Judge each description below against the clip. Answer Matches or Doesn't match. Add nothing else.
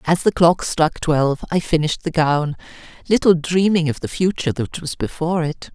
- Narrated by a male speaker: Doesn't match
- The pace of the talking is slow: Doesn't match